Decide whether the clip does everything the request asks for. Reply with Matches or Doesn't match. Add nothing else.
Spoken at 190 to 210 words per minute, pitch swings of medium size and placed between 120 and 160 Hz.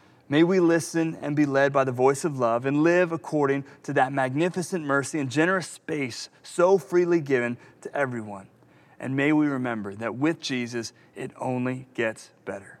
Doesn't match